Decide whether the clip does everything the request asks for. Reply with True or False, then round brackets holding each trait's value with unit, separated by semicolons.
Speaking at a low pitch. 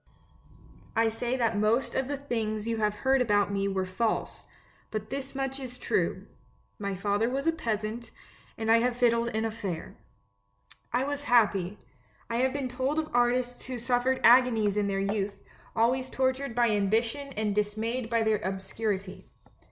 False (230 Hz)